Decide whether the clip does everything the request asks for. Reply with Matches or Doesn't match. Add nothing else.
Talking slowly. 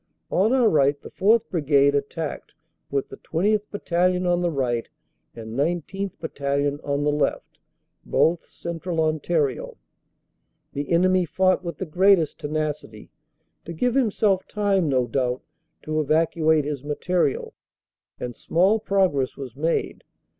Matches